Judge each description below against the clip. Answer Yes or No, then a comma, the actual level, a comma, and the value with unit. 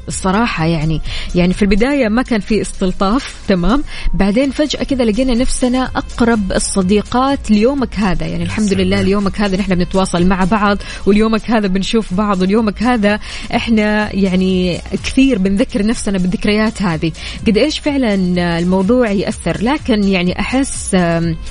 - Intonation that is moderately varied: Yes, average, 3.9 semitones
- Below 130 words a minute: No, fast, 135 wpm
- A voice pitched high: Yes, high, 210 Hz